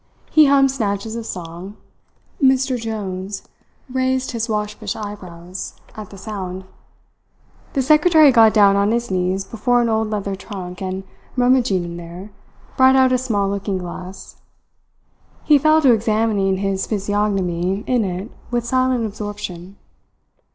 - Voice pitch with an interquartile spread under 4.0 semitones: No, average, 4.3 semitones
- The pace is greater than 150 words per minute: No, slow, 135 wpm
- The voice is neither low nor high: No, high, 210 Hz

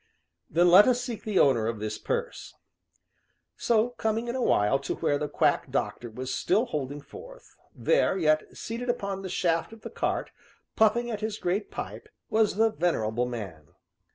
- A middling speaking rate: Yes, average, 175 wpm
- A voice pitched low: No, high, 190 Hz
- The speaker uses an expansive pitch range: Yes, wide, 8.7 semitones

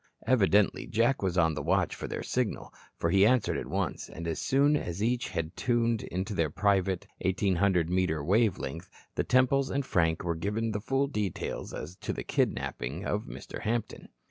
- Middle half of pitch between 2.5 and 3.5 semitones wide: No, wide, 5.5 semitones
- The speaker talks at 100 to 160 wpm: No, average, 185 wpm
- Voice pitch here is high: No, low, 100 Hz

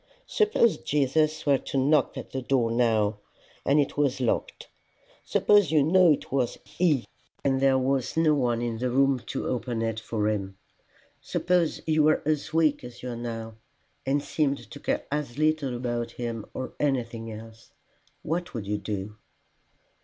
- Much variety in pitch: No, average, 4.3 semitones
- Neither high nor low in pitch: No, low, 130 Hz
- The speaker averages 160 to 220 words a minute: Yes, average, 170 wpm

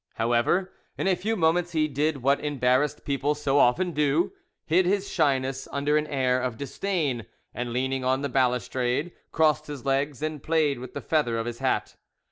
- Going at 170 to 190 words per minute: Yes, average, 180 wpm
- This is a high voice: No, medium, 140 Hz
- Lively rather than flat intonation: No, average, 3.4 semitones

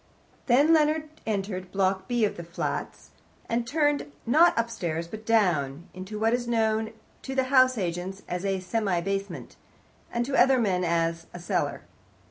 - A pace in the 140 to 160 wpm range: Yes, average, 155 wpm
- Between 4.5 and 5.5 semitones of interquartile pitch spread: Yes, average, 5.0 semitones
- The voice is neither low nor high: No, high, 215 Hz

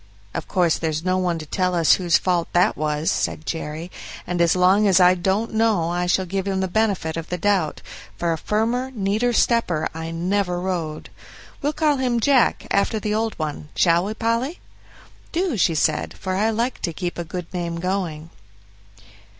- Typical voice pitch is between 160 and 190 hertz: Yes, medium, 185 Hz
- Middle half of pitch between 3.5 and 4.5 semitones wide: Yes, average, 4.2 semitones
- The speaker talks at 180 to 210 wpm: Yes, average, 190 wpm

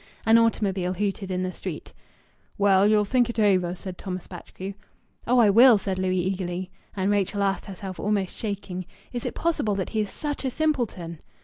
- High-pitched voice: Yes, high, 195 Hz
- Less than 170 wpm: No, average, 185 wpm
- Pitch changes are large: No, average, 2.9 semitones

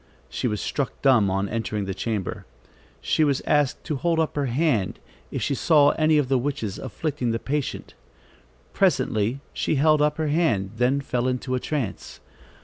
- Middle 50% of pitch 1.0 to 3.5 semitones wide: No, average, 4.7 semitones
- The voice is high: No, low, 135 Hz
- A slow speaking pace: No, average, 175 wpm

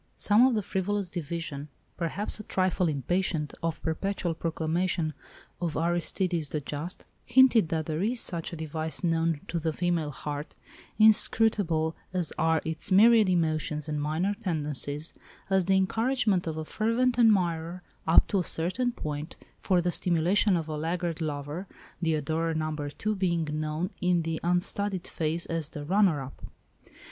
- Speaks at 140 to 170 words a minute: Yes, average, 150 wpm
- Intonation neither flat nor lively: Yes, average, 3.4 semitones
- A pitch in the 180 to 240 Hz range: No, medium, 170 Hz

